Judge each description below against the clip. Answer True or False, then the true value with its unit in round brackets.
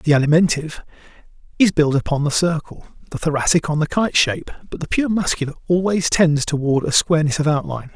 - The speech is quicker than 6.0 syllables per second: True (6.3 syllables/s)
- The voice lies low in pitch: False (160 Hz)